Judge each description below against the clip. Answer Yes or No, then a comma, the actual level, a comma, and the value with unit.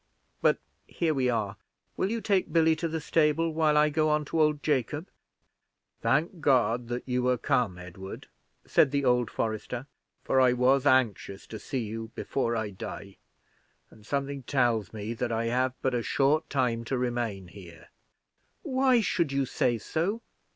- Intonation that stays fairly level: No, average, 4.8 semitones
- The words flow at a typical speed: Yes, average, 170 wpm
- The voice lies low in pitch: Yes, low, 130 Hz